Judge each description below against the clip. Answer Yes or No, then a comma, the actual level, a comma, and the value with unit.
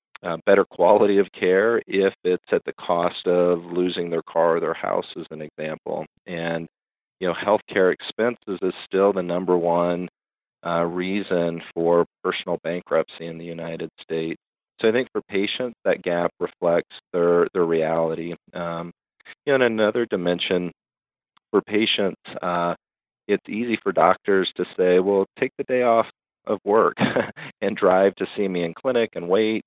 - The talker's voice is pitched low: Yes, very low, 90 Hz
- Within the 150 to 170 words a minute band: Yes, average, 160 wpm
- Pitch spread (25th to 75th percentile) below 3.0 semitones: Yes, narrow, 2.6 semitones